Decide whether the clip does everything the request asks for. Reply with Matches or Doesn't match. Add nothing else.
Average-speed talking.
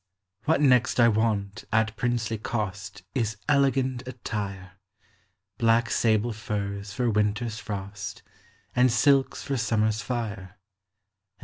Doesn't match